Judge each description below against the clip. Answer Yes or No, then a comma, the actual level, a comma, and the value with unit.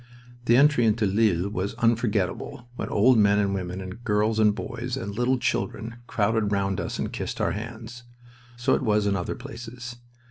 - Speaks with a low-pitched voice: Yes, low, 110 Hz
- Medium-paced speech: Yes, average, 180 wpm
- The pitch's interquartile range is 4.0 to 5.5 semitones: No, average, 2.9 semitones